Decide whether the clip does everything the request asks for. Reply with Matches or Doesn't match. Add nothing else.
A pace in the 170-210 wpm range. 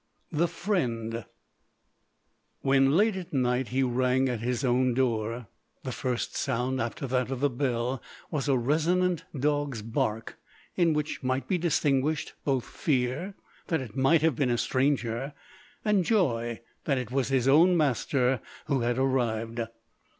Doesn't match